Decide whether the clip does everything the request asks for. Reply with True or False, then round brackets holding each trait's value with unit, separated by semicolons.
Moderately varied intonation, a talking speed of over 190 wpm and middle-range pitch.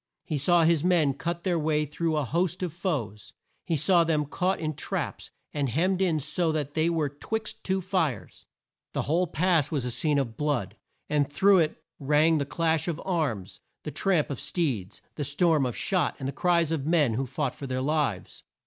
True (3.4 semitones; 200 wpm; 155 Hz)